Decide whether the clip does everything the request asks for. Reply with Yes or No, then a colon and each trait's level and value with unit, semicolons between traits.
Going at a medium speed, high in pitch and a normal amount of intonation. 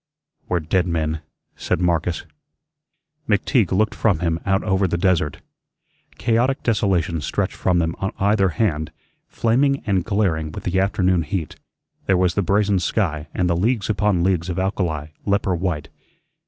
No: average, 155 wpm; very low, 95 Hz; average, 3.2 semitones